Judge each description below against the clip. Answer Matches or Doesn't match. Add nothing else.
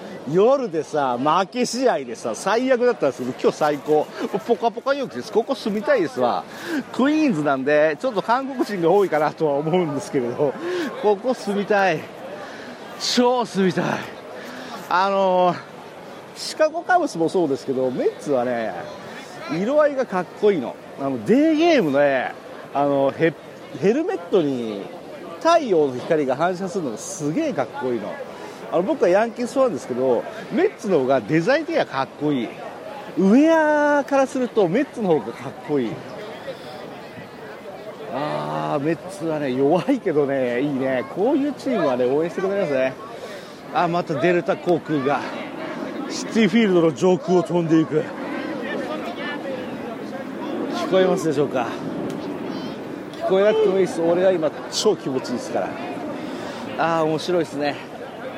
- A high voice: Matches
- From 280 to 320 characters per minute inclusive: Matches